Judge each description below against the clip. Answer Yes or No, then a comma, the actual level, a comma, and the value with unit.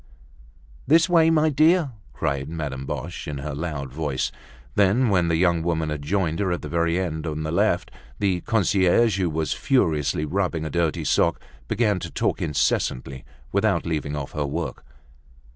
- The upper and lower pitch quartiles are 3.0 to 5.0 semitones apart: Yes, average, 4.7 semitones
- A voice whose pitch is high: No, very low, 85 Hz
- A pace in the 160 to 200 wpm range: Yes, average, 170 wpm